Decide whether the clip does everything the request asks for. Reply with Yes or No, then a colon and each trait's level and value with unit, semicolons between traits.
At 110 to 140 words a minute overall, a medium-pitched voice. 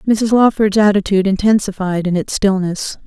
No: slow, 135 wpm; high, 200 Hz